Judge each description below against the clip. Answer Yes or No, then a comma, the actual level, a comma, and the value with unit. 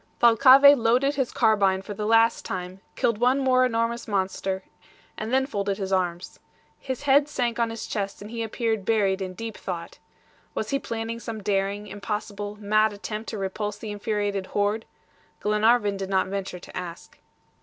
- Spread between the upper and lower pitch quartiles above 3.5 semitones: No, average, 2.8 semitones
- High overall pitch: Yes, high, 210 Hz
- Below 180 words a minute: Yes, average, 170 wpm